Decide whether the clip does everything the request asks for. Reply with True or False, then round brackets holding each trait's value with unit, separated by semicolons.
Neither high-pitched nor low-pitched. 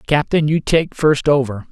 True (145 Hz)